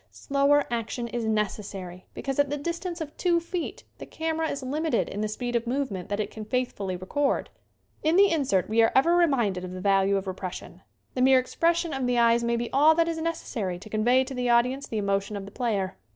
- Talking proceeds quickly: Yes, fast, 225 wpm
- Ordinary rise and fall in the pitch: No, wide, 6.0 semitones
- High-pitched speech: Yes, high, 245 Hz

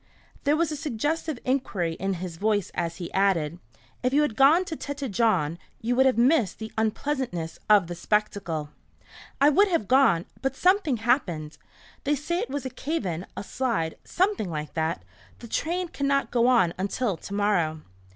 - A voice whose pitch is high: Yes, high, 230 Hz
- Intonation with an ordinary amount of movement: No, wide, 8.1 semitones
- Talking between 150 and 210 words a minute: Yes, average, 180 wpm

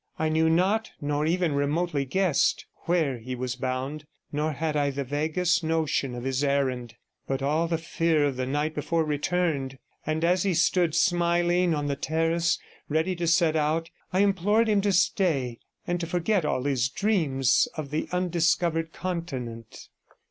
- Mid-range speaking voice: Yes, medium, 160 Hz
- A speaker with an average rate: Yes, average, 165 wpm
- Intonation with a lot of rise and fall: No, average, 3.7 semitones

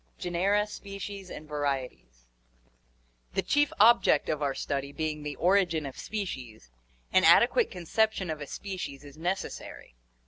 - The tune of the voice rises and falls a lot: Yes, wide, 6.2 semitones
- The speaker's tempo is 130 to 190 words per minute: Yes, average, 140 wpm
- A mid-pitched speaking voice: Yes, medium, 160 Hz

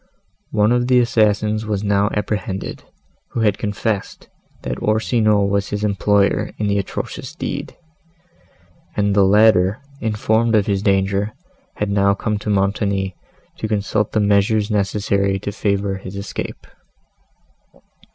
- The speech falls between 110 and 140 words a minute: Yes, slow, 135 wpm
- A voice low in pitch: Yes, low, 105 Hz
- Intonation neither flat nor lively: No, narrow, 1.4 semitones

